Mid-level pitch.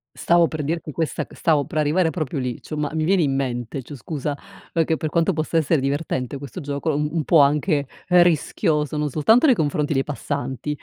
Yes: medium, 150 Hz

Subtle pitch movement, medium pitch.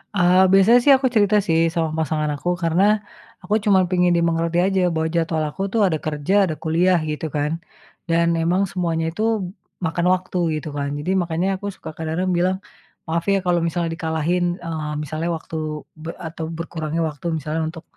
Yes: narrow, 2.2 semitones; medium, 165 Hz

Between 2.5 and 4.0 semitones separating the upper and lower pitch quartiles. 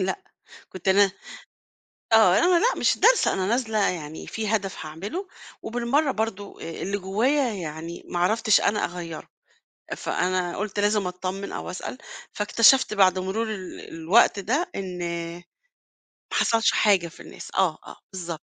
Yes: average, 3.6 semitones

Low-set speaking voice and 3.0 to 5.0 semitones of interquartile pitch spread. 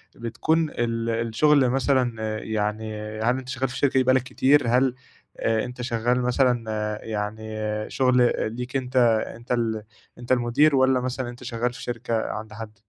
No: low, 120 Hz; narrow, 2.4 semitones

